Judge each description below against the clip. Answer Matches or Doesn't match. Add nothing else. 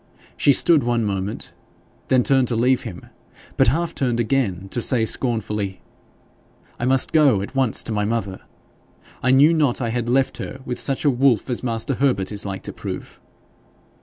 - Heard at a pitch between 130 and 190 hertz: Doesn't match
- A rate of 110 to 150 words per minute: Doesn't match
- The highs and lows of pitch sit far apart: Doesn't match